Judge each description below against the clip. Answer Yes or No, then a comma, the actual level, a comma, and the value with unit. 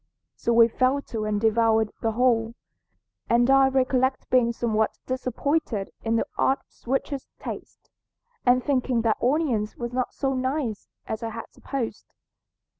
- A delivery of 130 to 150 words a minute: Yes, average, 145 wpm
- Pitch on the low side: No, high, 240 Hz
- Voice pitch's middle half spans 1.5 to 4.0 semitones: Yes, narrow, 2.6 semitones